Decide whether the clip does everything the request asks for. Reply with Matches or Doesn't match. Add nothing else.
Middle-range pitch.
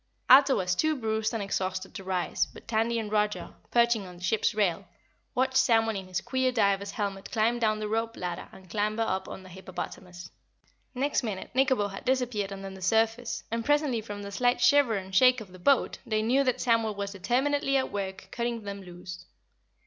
Doesn't match